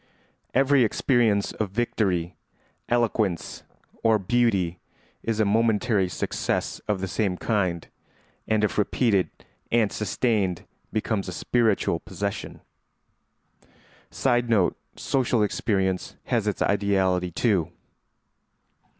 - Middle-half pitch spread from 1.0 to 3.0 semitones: No, average, 3.6 semitones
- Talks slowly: Yes, slow, 100 wpm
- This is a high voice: No, low, 105 Hz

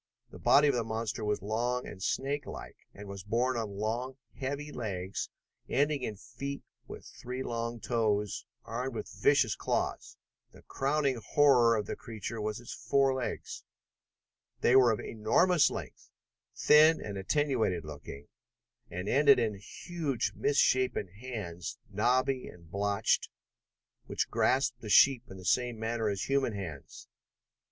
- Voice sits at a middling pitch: No, low, 115 Hz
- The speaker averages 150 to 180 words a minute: No, average, 140 wpm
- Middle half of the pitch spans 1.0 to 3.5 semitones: No, average, 4.3 semitones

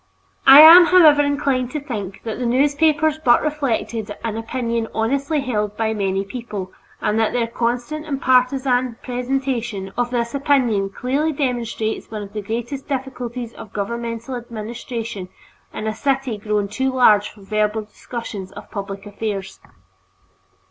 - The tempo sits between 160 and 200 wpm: No, average, 145 wpm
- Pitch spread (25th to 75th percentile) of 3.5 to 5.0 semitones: Yes, average, 4.0 semitones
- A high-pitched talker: Yes, high, 235 Hz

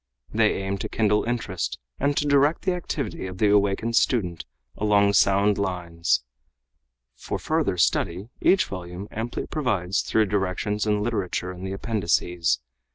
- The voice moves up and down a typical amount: Yes, average, 3.8 semitones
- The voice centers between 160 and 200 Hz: No, low, 100 Hz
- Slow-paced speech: No, average, 145 wpm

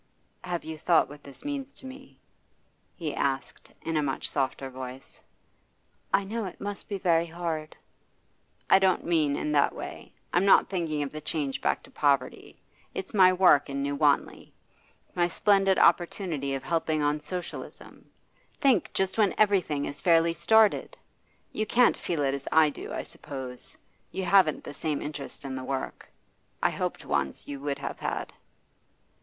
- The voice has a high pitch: No, medium, 160 Hz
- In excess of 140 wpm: Yes, average, 165 wpm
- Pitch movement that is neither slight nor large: Yes, average, 5.0 semitones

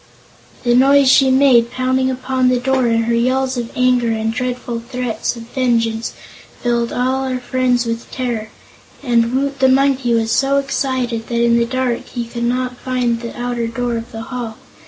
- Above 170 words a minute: Yes, average, 180 wpm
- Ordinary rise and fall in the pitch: No, narrow, 1.8 semitones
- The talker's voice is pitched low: No, high, 245 Hz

